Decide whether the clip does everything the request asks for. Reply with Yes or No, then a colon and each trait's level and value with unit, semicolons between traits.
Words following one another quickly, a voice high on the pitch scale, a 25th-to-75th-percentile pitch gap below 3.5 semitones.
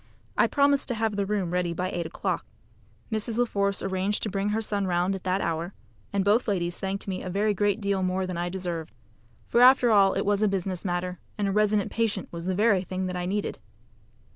Yes: fast, 225 wpm; high, 195 Hz; narrow, 2.4 semitones